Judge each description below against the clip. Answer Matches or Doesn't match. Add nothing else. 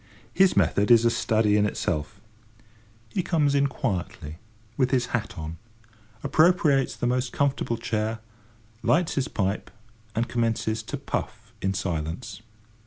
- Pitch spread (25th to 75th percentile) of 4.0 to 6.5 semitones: Matches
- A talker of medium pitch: Doesn't match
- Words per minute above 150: Doesn't match